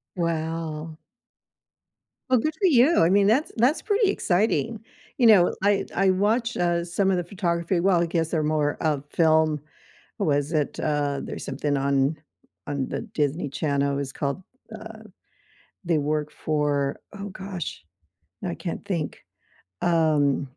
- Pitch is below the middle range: No, medium, 165 Hz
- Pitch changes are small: No, average, 5.0 semitones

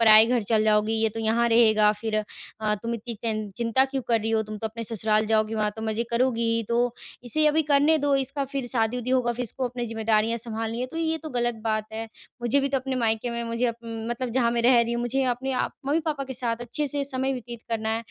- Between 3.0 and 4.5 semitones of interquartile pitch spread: No, narrow, 2.6 semitones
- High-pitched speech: Yes, high, 235 Hz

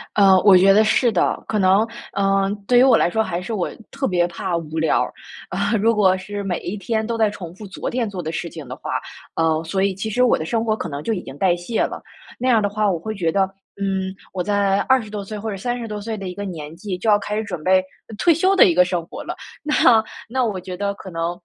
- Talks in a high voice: Yes, high, 195 Hz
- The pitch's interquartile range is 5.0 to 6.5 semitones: No, average, 3.4 semitones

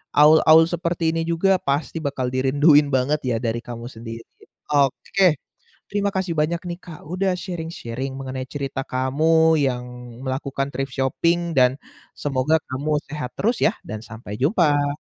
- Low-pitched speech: No, medium, 145 Hz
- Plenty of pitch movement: No, average, 4.0 semitones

